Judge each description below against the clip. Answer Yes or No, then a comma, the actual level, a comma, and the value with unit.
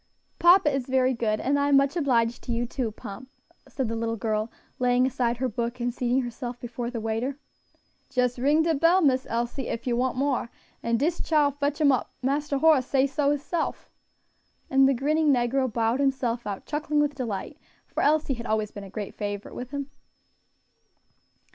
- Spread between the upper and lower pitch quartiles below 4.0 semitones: Yes, average, 3.2 semitones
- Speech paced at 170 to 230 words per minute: Yes, average, 190 wpm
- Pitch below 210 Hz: No, very high, 255 Hz